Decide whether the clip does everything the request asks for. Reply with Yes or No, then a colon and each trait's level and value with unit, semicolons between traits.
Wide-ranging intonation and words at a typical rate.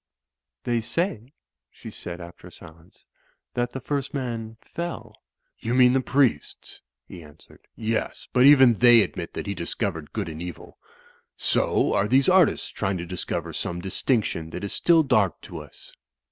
Yes: wide, 6.5 semitones; average, 160 wpm